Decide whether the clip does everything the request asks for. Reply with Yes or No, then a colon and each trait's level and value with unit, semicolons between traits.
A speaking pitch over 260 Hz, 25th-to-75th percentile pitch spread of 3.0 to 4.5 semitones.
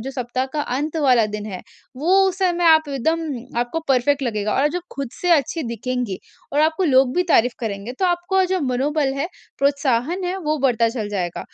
No: very high, 275 Hz; average, 5.2 semitones